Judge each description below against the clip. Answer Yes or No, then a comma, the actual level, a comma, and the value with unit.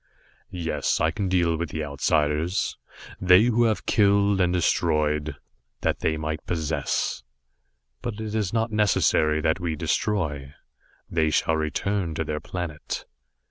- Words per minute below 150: Yes, average, 140 wpm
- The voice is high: No, very low, 85 Hz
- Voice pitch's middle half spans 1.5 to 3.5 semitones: No, average, 4.5 semitones